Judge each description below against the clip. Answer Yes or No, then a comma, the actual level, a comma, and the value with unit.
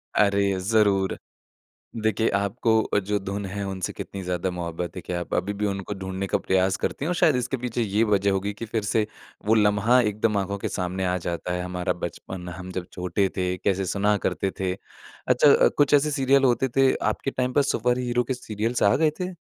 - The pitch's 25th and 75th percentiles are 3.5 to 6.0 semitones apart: Yes, average, 3.9 semitones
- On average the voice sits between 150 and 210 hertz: No, low, 100 Hz